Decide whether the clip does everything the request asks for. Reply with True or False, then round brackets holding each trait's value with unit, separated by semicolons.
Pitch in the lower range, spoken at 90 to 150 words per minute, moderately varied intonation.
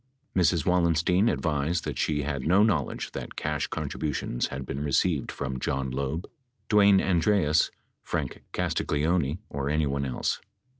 True (75 Hz; 140 wpm; 4.2 semitones)